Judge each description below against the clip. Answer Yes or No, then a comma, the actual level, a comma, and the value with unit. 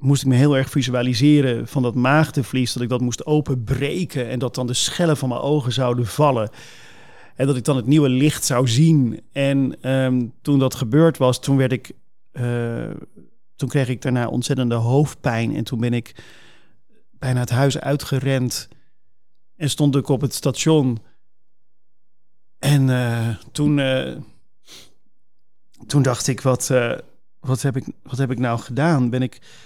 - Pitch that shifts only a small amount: Yes, narrow, 2.3 semitones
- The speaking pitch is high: No, low, 130 Hz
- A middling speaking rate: Yes, average, 165 wpm